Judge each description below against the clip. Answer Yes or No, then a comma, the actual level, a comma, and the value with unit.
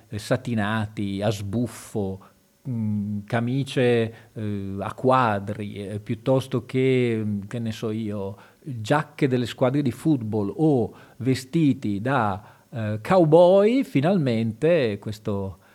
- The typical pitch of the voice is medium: No, low, 115 Hz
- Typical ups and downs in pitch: Yes, average, 4.0 semitones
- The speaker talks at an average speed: No, slow, 90 wpm